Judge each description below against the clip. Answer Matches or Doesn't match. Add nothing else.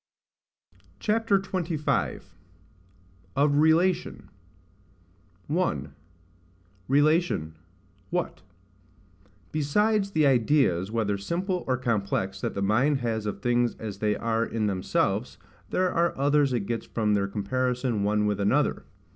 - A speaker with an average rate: Doesn't match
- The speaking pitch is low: Matches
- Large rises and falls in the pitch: Matches